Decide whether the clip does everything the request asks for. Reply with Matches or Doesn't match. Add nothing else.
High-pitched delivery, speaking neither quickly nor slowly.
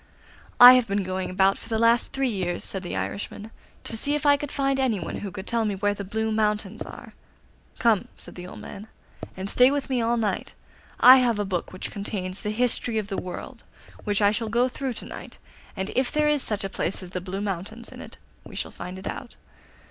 Doesn't match